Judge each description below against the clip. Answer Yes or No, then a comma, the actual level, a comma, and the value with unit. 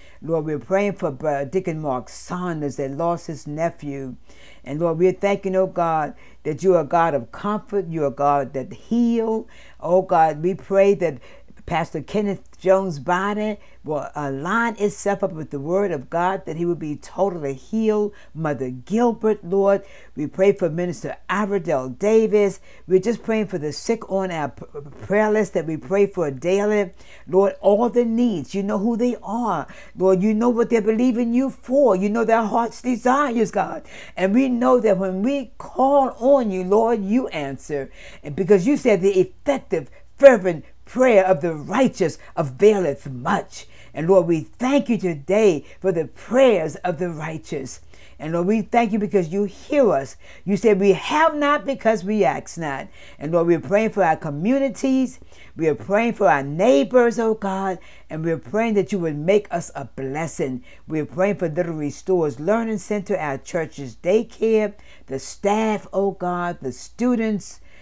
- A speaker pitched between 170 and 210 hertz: Yes, high, 190 Hz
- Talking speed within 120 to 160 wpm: No, average, 180 wpm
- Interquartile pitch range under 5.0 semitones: No, wide, 5.4 semitones